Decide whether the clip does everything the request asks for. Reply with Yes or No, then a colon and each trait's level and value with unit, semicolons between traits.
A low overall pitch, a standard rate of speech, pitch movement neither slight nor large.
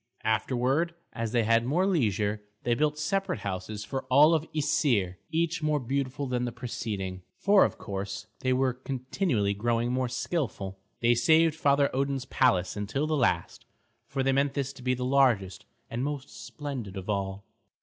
Yes: low, 125 Hz; average, 170 wpm; average, 4.8 semitones